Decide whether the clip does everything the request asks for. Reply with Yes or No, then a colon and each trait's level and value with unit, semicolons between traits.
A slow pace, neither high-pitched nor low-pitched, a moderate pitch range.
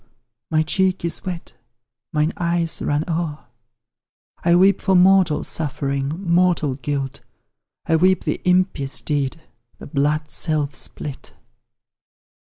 Yes: slow, 115 wpm; medium, 160 Hz; average, 3.5 semitones